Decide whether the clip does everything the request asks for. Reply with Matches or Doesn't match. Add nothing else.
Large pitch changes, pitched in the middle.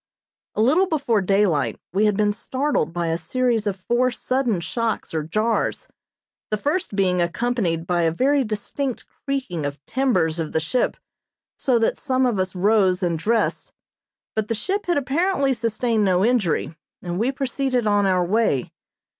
Doesn't match